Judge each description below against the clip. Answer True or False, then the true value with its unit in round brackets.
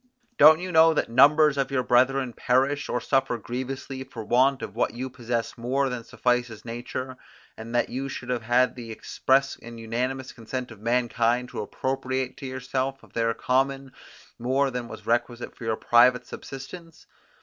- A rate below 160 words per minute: False (170 wpm)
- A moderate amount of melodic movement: False (2.1 semitones)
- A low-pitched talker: True (125 Hz)